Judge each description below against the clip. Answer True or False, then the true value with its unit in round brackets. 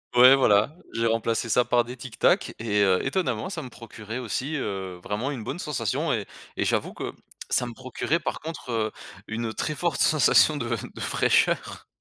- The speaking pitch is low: True (120 Hz)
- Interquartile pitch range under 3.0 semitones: False (3.5 semitones)